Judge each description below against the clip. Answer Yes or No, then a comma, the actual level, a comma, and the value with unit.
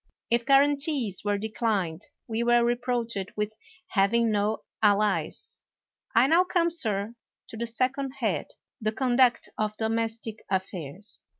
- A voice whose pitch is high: Yes, high, 225 Hz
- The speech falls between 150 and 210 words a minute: No, slow, 135 wpm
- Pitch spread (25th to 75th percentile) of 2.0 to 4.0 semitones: Yes, average, 3.1 semitones